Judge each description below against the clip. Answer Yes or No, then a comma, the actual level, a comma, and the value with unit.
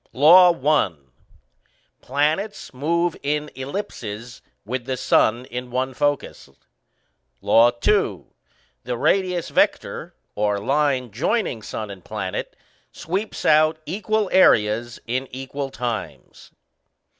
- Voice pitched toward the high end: No, low, 135 Hz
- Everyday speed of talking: No, slow, 105 wpm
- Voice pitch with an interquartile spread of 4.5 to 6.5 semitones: Yes, wide, 5.4 semitones